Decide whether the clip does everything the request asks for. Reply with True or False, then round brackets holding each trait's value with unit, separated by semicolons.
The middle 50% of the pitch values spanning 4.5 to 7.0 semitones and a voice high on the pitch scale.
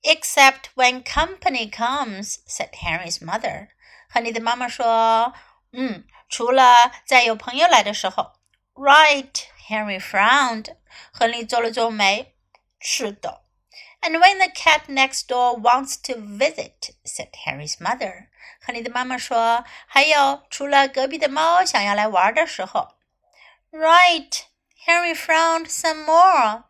True (5.3 semitones; 265 Hz)